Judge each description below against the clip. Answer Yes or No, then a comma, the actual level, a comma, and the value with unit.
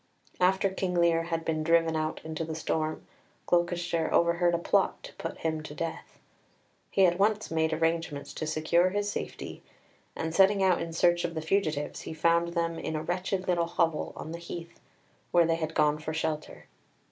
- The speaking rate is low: No, average, 185 wpm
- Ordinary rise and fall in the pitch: No, narrow, 1.6 semitones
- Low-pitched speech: No, medium, 165 Hz